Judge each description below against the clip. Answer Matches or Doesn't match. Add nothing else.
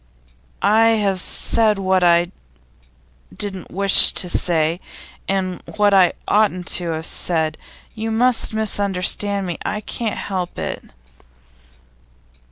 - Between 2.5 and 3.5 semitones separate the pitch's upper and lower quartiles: Matches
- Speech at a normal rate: Doesn't match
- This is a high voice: Matches